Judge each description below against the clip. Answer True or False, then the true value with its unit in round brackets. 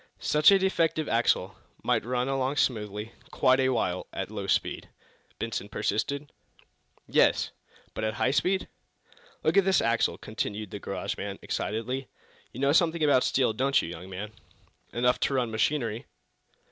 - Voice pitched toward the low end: True (125 Hz)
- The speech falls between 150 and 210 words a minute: True (160 wpm)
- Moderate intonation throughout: True (4.8 semitones)